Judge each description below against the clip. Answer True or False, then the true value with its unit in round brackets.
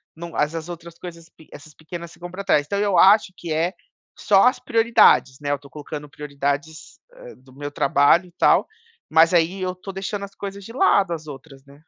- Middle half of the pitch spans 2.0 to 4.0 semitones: False (4.6 semitones)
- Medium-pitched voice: True (165 Hz)